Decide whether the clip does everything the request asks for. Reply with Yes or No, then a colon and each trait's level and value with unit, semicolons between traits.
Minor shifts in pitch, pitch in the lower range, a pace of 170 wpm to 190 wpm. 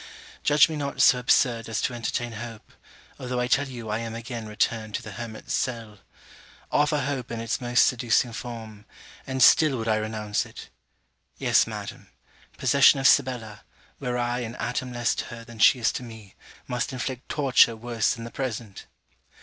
Yes: narrow, 2.1 semitones; low, 120 Hz; average, 180 wpm